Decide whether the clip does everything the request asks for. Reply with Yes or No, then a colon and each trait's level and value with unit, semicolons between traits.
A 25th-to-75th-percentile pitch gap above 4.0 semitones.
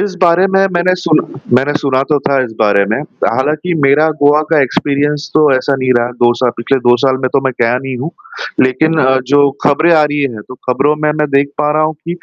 No: average, 3.1 semitones